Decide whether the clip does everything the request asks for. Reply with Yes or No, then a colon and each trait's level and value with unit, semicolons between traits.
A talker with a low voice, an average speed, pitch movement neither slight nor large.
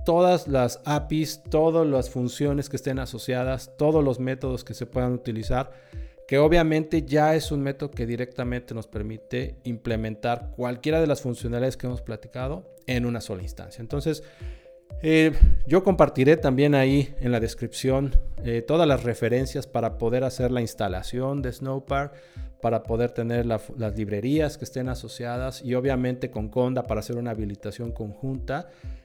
Yes: low, 125 Hz; average, 155 wpm; average, 3.2 semitones